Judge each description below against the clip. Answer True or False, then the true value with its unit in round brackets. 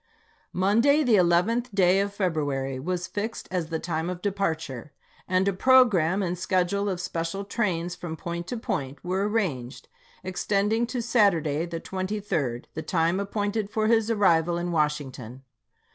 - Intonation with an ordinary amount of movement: True (3.9 semitones)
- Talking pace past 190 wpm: False (155 wpm)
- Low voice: False (185 Hz)